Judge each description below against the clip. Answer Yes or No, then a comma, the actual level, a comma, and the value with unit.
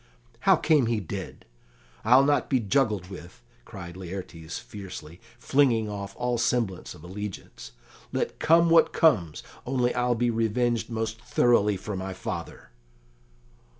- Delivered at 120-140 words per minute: Yes, slow, 135 wpm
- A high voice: No, low, 110 Hz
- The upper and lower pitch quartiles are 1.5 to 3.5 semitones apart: No, average, 4.6 semitones